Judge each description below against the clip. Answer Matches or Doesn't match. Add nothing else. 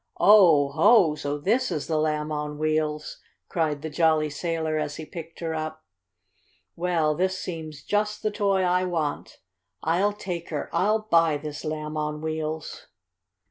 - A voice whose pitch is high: Doesn't match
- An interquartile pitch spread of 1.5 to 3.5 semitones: Matches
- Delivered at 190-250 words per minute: Doesn't match